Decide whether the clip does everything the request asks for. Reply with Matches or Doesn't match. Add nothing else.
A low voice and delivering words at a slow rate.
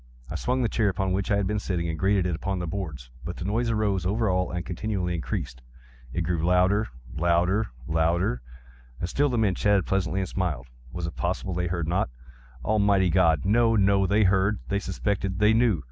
Doesn't match